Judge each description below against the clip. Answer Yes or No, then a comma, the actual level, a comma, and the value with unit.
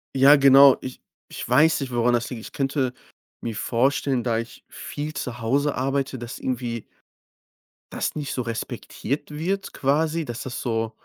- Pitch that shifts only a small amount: No, average, 3.0 semitones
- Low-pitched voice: Yes, low, 130 Hz